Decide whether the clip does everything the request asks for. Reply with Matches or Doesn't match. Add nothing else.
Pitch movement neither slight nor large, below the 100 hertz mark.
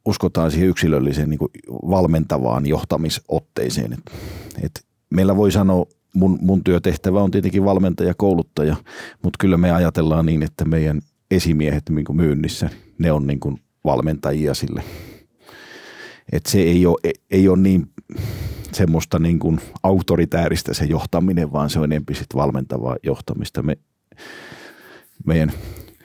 Matches